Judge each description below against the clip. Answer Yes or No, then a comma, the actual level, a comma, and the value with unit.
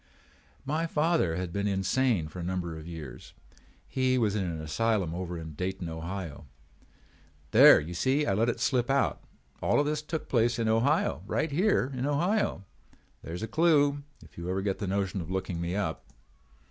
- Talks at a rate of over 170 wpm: Yes, average, 190 wpm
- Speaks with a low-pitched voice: Yes, low, 100 Hz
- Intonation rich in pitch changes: Yes, wide, 7.7 semitones